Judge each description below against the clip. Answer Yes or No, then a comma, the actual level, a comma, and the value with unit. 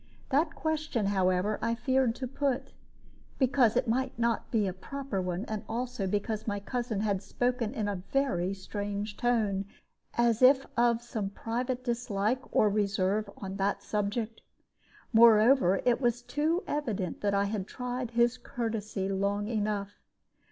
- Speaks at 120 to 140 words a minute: No, average, 150 wpm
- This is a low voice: No, high, 225 Hz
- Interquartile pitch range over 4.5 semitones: No, average, 3.5 semitones